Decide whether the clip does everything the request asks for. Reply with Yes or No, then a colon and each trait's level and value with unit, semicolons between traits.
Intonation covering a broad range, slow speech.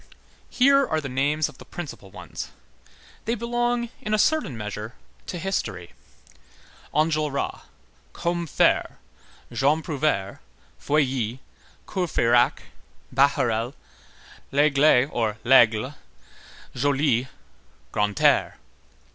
Yes: wide, 6.1 semitones; slow, 90 wpm